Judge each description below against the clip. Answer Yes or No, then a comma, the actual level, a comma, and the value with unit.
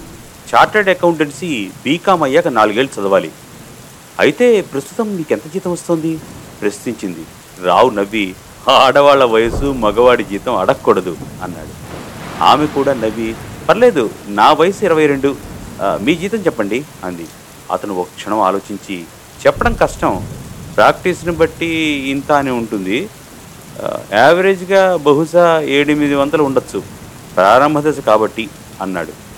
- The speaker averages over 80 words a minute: Yes, average, 105 wpm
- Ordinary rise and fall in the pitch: No, wide, 7.1 semitones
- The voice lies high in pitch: No, medium, 140 Hz